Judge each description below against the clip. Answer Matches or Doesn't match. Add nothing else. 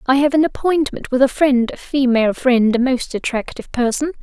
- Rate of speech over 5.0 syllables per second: Matches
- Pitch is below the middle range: Doesn't match